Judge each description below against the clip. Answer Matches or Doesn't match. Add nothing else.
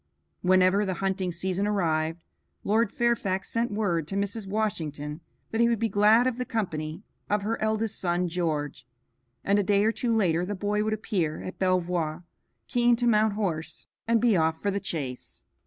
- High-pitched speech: Matches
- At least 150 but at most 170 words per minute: Doesn't match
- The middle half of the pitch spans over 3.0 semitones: Matches